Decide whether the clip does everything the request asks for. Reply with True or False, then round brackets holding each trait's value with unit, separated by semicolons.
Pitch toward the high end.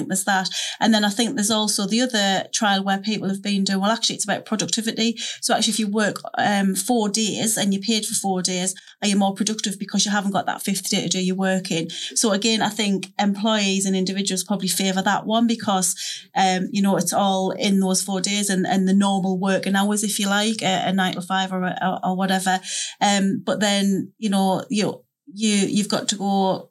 True (200 Hz)